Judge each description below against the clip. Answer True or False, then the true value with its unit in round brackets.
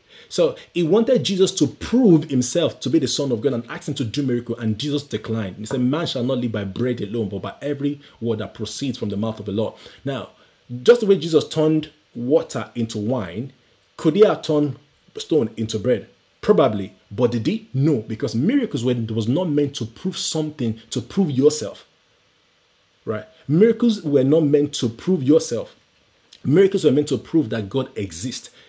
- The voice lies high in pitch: False (140 Hz)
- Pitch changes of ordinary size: False (6.0 semitones)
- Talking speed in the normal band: True (190 wpm)